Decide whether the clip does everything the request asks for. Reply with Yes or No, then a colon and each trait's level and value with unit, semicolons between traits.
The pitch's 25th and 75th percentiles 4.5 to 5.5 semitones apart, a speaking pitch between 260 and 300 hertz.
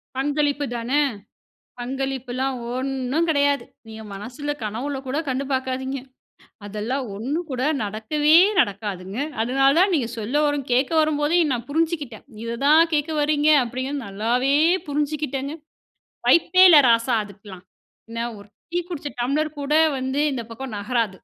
No: average, 4.0 semitones; very high, 265 Hz